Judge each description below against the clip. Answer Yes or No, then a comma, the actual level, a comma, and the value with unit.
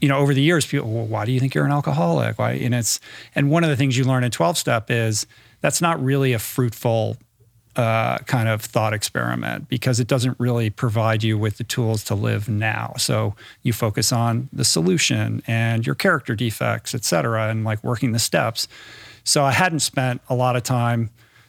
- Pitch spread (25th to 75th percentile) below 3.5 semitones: Yes, average, 2.8 semitones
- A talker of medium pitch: No, low, 120 Hz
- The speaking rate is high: Yes, fast, 210 wpm